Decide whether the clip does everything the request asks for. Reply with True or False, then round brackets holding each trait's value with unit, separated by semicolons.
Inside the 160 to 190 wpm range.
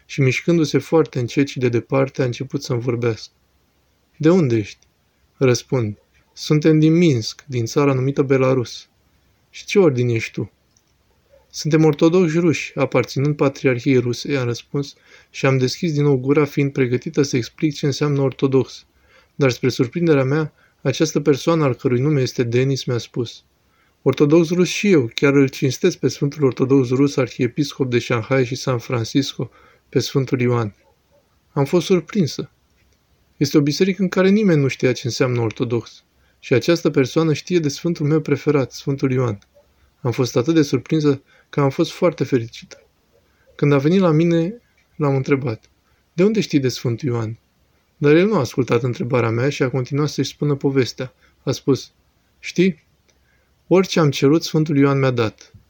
True (165 wpm)